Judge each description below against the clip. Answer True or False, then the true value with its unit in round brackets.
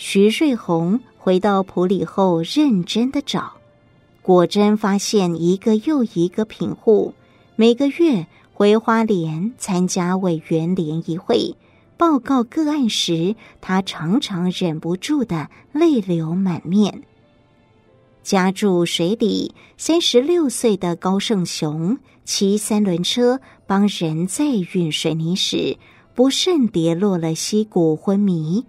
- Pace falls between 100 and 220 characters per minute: True (175 characters per minute)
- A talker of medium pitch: False (195 Hz)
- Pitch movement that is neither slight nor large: True (5.0 semitones)